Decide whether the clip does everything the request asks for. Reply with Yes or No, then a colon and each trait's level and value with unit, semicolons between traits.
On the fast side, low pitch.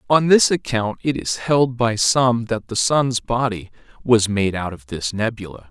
No: average, 190 wpm; low, 115 Hz